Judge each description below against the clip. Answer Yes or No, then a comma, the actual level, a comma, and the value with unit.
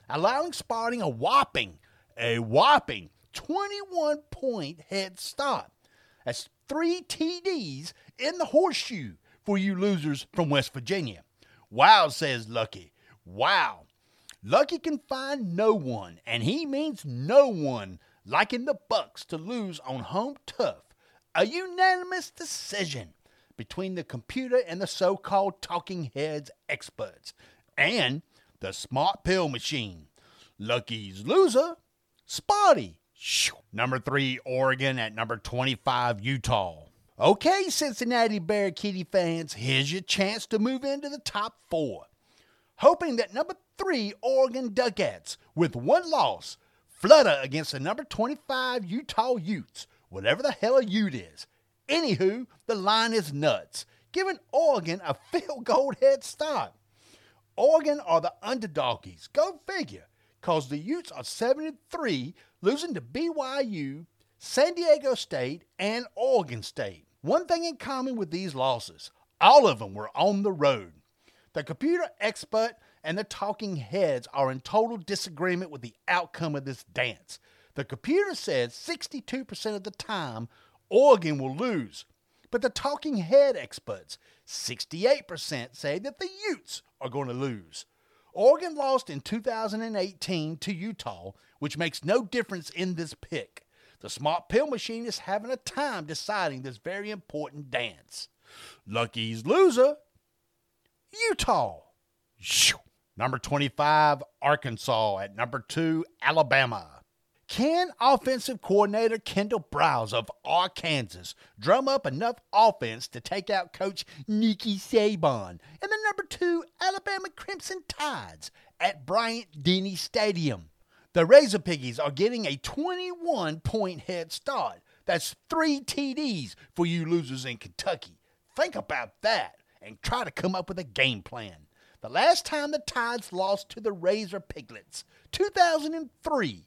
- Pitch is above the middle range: Yes, high, 200 Hz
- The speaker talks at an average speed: No, slow, 130 wpm